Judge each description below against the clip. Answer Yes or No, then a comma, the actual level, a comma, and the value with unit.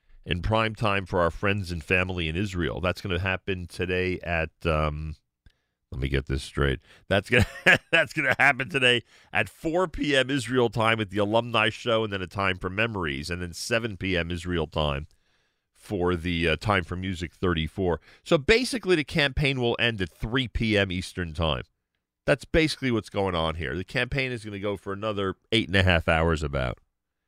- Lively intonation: No, average, 4.9 semitones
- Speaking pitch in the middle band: No, very low, 95 Hz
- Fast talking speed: No, average, 195 wpm